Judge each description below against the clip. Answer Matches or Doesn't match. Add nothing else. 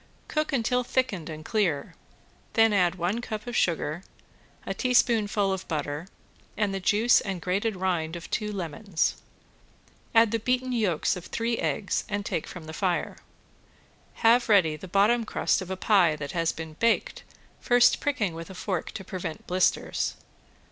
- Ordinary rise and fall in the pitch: Matches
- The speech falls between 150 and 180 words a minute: Matches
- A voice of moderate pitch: Doesn't match